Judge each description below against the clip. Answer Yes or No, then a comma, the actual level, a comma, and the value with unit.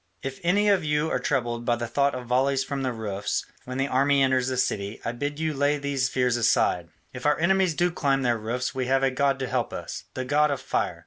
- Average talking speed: No, fast, 245 wpm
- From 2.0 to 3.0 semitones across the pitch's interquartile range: Yes, average, 2.7 semitones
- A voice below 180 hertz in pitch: Yes, low, 135 Hz